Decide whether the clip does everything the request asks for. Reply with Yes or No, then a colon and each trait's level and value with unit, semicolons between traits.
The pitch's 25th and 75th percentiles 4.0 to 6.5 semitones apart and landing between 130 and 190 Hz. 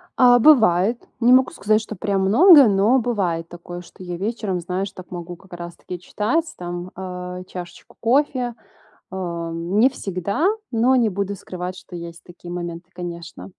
Yes: average, 4.3 semitones; medium, 185 Hz